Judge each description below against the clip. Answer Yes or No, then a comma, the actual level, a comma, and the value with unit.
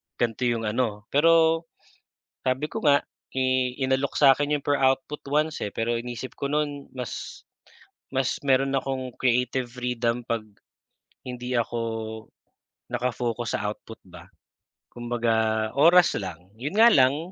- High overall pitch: No, low, 130 Hz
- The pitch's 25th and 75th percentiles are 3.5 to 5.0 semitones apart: No, average, 3.1 semitones